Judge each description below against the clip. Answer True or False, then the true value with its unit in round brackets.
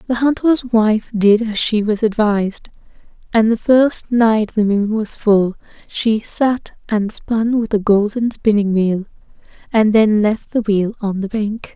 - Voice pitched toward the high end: True (215 Hz)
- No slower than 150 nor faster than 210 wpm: True (170 wpm)